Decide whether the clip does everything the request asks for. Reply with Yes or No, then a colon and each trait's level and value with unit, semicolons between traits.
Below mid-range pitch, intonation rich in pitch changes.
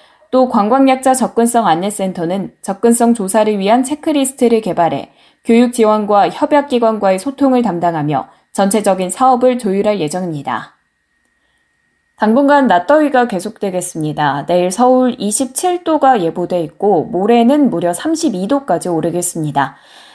No: high, 215 Hz; wide, 6.3 semitones